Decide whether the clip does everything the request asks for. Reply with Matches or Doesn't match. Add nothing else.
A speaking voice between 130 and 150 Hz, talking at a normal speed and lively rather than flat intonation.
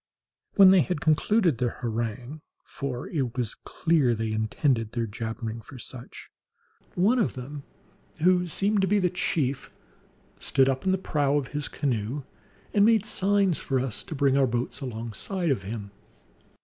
Matches